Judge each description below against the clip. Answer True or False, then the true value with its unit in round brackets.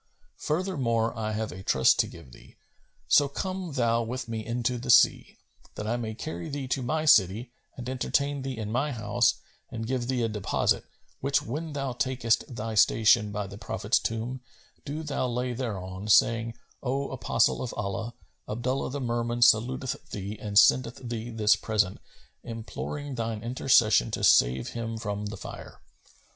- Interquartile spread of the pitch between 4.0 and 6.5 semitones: False (3.2 semitones)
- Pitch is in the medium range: False (115 Hz)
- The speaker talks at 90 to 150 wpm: False (165 wpm)